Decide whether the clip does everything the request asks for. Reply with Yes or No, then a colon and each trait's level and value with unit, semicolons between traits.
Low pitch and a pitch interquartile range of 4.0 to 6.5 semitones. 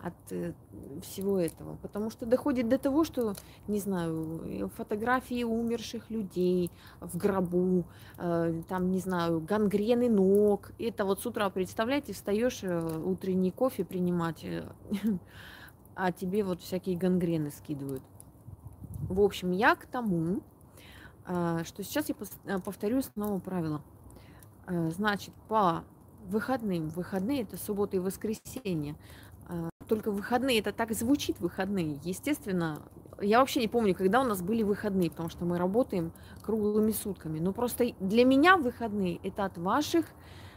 No: high, 195 Hz; average, 4.7 semitones